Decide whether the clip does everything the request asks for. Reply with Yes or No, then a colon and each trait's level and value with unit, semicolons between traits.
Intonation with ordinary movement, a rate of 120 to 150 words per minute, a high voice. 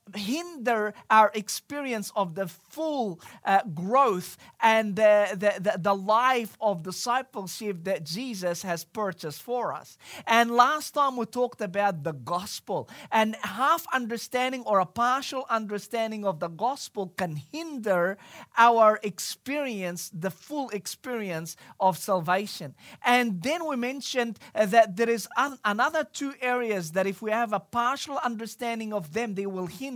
Yes: average, 4.3 semitones; average, 140 wpm; high, 215 Hz